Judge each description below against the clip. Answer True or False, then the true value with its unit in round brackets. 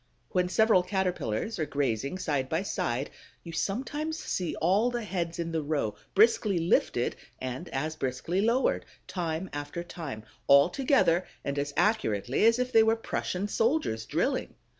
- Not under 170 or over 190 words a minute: False (155 wpm)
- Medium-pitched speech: True (175 Hz)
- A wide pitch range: True (7.1 semitones)